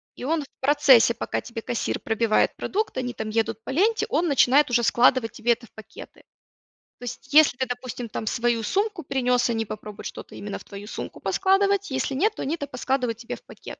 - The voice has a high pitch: Yes, very high, 250 Hz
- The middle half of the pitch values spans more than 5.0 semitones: No, average, 4.2 semitones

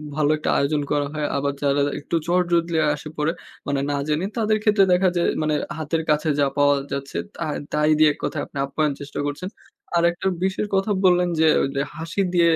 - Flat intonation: No, average, 3.5 semitones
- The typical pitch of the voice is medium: Yes, medium, 155 Hz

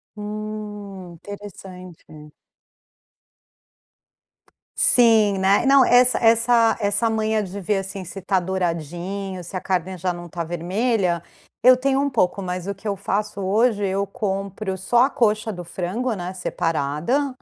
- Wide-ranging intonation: No, average, 3.4 semitones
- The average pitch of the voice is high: Yes, high, 200 Hz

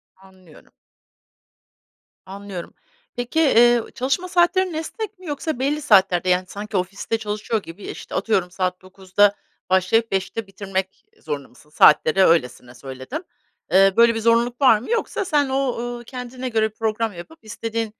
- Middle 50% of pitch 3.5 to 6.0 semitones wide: Yes, average, 5.1 semitones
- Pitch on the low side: No, high, 220 Hz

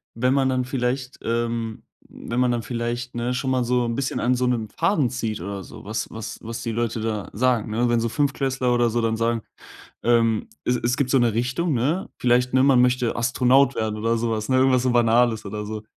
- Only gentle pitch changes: Yes, narrow, 1.8 semitones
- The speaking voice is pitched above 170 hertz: No, low, 120 Hz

